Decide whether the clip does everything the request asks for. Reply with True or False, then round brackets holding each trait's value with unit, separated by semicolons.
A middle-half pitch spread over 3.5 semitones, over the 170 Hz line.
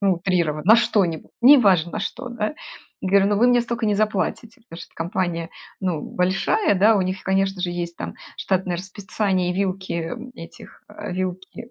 False (3.0 semitones; 190 Hz)